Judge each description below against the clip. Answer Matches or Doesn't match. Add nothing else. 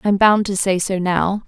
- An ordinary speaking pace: Doesn't match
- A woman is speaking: Matches